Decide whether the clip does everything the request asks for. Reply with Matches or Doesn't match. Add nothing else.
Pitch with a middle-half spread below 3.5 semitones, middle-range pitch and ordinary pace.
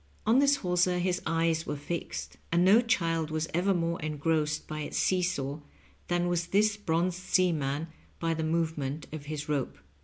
Matches